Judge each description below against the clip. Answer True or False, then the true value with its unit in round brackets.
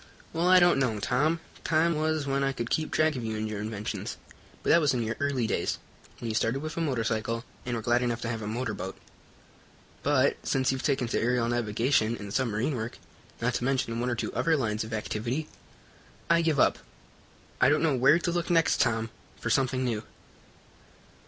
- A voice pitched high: False (125 Hz)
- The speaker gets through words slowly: False (205 wpm)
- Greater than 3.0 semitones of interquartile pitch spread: True (4.5 semitones)